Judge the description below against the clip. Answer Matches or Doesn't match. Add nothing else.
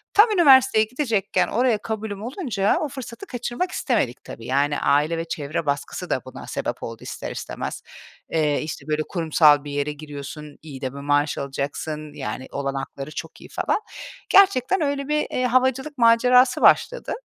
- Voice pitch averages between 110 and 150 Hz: Doesn't match